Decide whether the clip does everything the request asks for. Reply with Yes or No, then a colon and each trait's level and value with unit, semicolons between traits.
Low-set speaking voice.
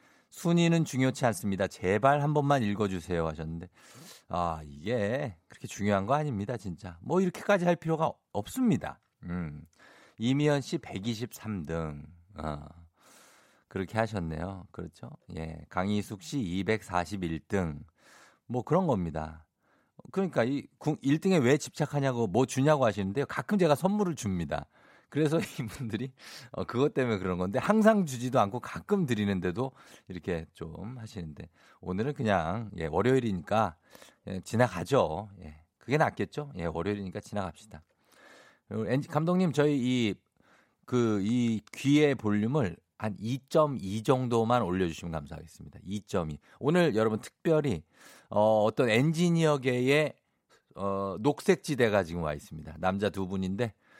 Yes: low, 110 Hz